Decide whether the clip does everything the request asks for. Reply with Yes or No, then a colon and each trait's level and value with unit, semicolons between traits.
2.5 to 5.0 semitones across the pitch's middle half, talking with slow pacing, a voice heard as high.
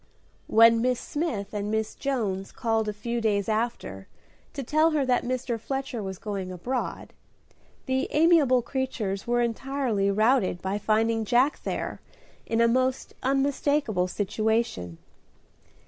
Yes: average, 4.1 semitones; slow, 130 wpm; high, 230 Hz